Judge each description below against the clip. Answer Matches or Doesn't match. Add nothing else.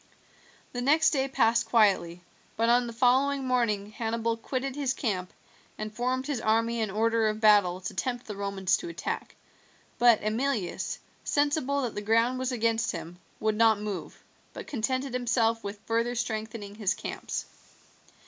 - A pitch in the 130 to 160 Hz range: Doesn't match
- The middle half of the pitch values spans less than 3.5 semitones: Matches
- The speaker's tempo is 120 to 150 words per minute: Doesn't match